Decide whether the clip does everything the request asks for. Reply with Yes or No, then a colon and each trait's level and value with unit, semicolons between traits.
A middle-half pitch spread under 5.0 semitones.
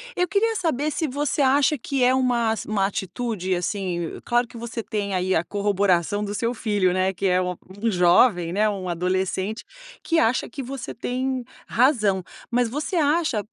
No: wide, 5.5 semitones